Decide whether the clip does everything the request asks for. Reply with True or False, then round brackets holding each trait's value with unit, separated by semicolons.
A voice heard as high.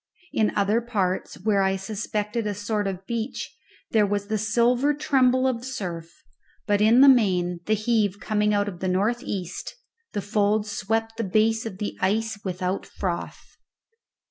True (210 Hz)